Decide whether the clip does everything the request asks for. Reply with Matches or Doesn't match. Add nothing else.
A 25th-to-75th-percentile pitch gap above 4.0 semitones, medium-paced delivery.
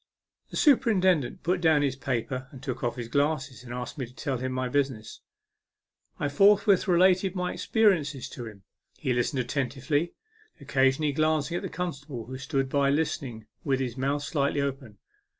Doesn't match